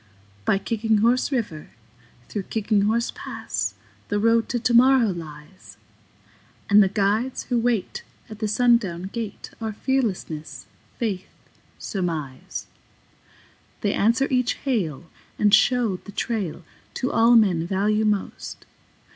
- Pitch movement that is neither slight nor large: Yes, average, 3.7 semitones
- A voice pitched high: Yes, high, 215 Hz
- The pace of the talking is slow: Yes, slow, 120 wpm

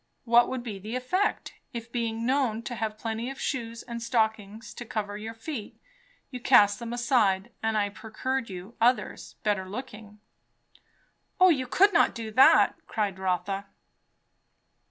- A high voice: Yes, high, 225 Hz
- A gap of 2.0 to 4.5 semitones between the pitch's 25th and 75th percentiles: Yes, average, 3.0 semitones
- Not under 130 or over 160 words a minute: Yes, average, 155 wpm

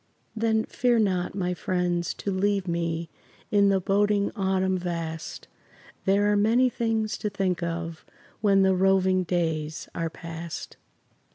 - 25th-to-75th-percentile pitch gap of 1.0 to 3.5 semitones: Yes, average, 3.0 semitones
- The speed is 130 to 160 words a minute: Yes, average, 140 wpm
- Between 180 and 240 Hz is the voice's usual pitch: Yes, high, 190 Hz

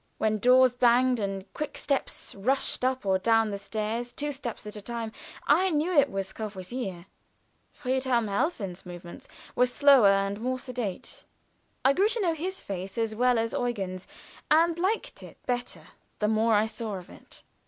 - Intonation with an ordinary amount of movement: Yes, average, 4.6 semitones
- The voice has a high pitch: Yes, high, 235 Hz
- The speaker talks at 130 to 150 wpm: No, average, 175 wpm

